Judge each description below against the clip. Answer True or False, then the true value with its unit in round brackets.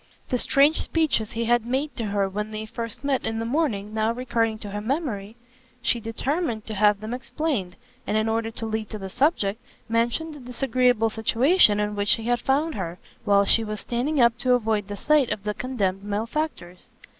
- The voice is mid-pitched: False (225 Hz)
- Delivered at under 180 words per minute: False (200 wpm)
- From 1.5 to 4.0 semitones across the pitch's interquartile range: True (3.5 semitones)